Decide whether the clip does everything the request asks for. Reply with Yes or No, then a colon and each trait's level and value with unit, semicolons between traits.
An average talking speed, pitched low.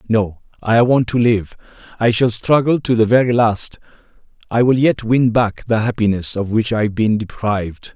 Yes: average, 190 wpm; low, 110 Hz